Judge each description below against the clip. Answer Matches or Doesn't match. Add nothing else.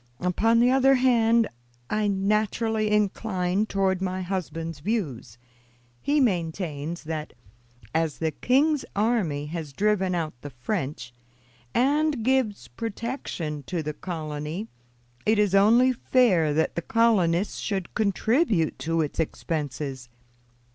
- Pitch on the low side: Doesn't match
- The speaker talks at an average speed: Doesn't match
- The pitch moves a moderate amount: Doesn't match